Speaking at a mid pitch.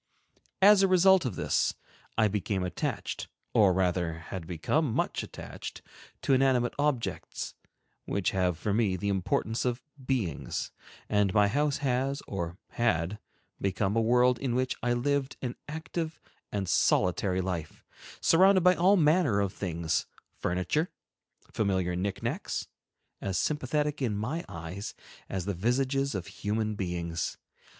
No: low, 110 Hz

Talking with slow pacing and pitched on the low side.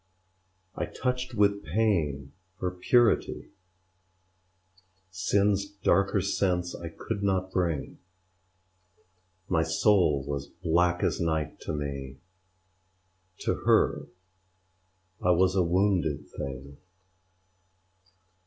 Yes: slow, 90 wpm; very low, 90 Hz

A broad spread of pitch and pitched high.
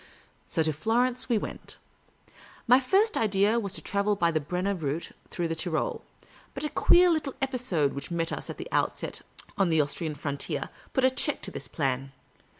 Yes: wide, 8.0 semitones; high, 195 Hz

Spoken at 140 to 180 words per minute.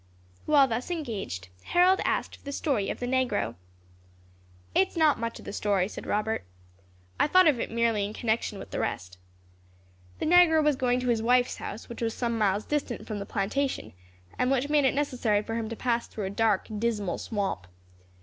No: average, 200 wpm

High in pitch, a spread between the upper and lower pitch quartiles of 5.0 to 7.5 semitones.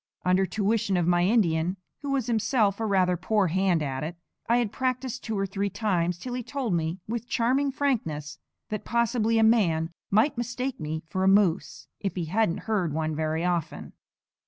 Yes: high, 200 Hz; average, 5.3 semitones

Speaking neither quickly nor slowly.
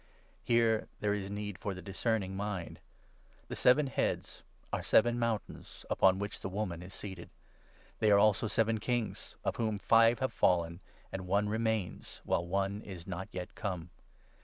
Yes: average, 170 wpm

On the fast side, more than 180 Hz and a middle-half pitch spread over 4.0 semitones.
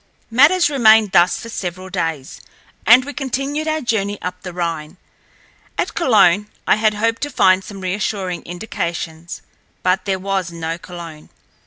No: average, 150 wpm; high, 190 Hz; average, 4.7 semitones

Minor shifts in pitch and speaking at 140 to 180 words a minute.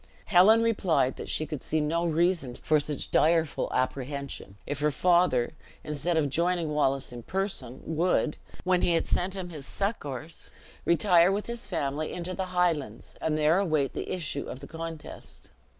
No: average, 3.7 semitones; average, 165 wpm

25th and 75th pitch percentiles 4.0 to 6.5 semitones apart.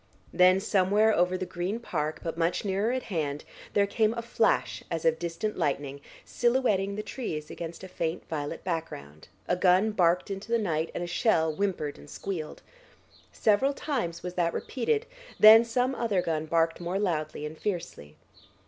Yes: average, 4.6 semitones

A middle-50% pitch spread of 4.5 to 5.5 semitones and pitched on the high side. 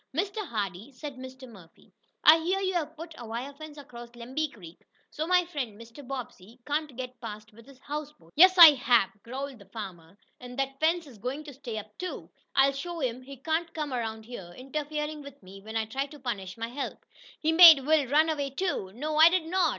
Yes: average, 5.1 semitones; very high, 270 Hz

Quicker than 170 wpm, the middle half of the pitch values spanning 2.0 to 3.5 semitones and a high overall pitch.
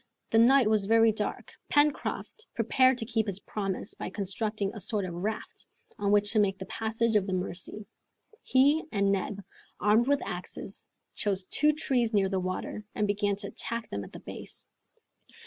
Yes: average, 180 wpm; narrow, 2.6 semitones; high, 210 Hz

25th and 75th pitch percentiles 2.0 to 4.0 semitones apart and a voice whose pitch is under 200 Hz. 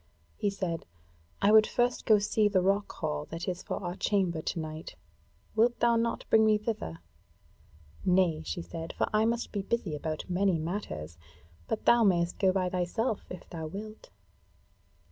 No: average, 4.4 semitones; high, 190 Hz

